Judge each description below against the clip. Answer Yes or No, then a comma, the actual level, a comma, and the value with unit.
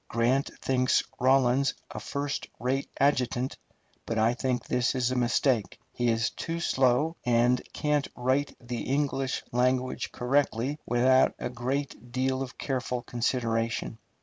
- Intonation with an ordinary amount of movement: No, narrow, 1.9 semitones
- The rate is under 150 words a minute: Yes, slow, 135 wpm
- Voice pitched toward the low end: Yes, low, 125 Hz